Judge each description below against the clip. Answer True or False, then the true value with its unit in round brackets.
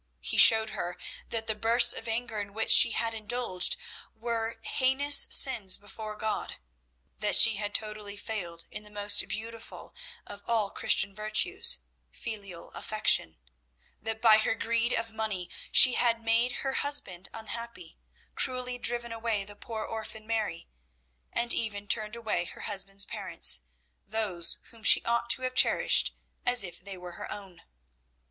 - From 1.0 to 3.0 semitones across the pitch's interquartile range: True (2.4 semitones)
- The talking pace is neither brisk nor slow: True (155 wpm)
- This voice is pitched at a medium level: False (220 Hz)